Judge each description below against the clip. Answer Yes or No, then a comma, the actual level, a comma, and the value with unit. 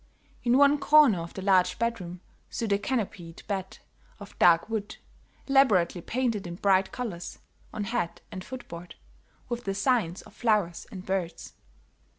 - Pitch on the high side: Yes, high, 200 Hz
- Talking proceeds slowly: No, average, 150 wpm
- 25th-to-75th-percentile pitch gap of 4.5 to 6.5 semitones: Yes, average, 5.0 semitones